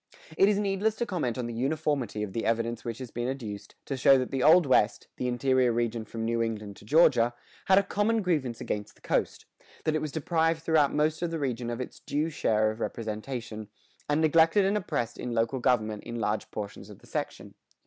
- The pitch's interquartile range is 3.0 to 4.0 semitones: No, wide, 5.6 semitones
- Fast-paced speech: Yes, fast, 220 wpm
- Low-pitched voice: Yes, low, 130 Hz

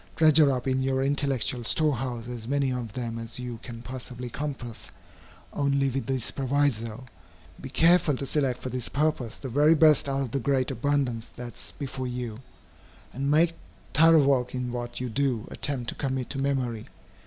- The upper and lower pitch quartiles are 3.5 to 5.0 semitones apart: No, narrow, 2.5 semitones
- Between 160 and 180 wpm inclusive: Yes, average, 175 wpm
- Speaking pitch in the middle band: No, low, 130 Hz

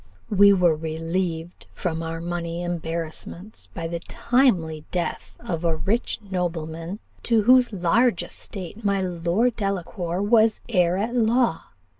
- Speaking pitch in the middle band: Yes, medium, 180 Hz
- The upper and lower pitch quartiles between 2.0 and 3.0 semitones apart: No, average, 4.1 semitones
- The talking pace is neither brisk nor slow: No, slow, 130 wpm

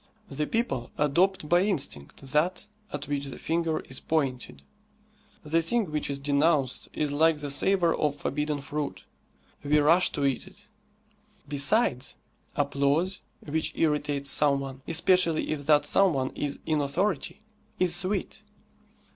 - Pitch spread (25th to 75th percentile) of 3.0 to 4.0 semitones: Yes, average, 3.3 semitones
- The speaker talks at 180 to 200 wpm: No, average, 140 wpm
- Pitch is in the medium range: Yes, medium, 150 Hz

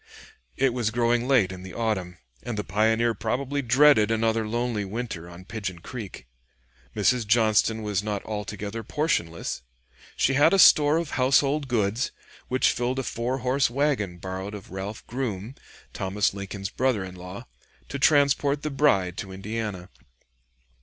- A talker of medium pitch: No, low, 110 Hz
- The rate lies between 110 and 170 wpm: Yes, average, 150 wpm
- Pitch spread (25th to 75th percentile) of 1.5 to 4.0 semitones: No, average, 4.6 semitones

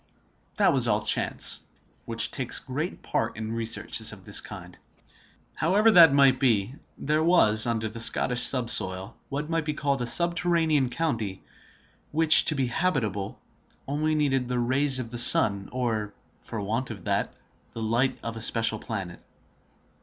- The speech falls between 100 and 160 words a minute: Yes, average, 155 wpm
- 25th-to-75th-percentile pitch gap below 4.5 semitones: No, average, 5.1 semitones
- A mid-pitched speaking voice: No, low, 125 Hz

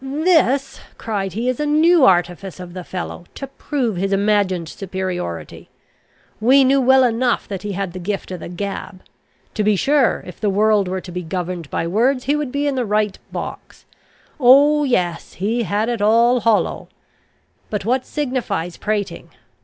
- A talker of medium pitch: No, high, 210 Hz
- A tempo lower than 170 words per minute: No, average, 175 wpm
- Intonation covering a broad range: Yes, wide, 5.7 semitones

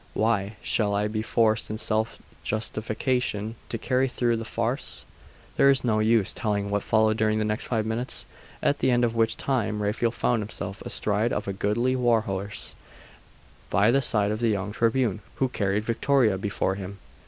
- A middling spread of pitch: No, narrow, 2.3 semitones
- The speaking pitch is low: Yes, low, 110 Hz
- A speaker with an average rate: Yes, average, 180 wpm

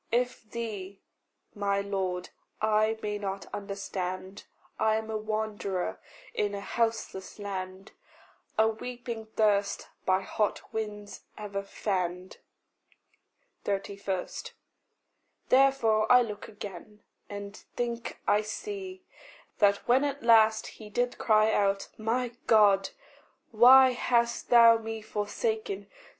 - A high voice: Yes, high, 215 Hz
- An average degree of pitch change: No, narrow, 2.3 semitones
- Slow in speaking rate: Yes, slow, 110 wpm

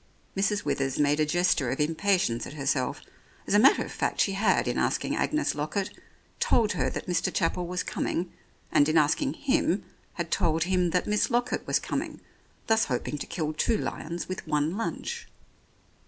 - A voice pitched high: No, medium, 175 Hz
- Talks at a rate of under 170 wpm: No, average, 180 wpm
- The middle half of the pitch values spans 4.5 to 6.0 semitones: Yes, average, 5.3 semitones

